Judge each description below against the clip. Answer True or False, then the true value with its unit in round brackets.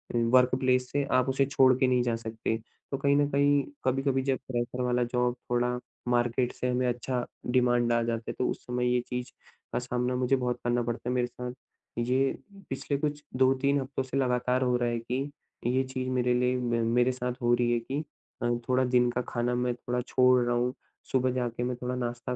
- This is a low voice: True (125 Hz)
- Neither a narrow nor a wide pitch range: False (1.0 semitones)